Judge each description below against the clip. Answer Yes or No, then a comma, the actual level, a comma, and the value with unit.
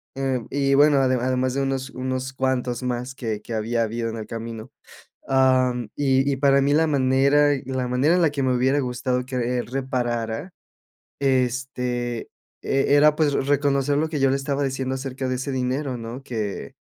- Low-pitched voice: Yes, low, 130 Hz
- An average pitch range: No, narrow, 1.8 semitones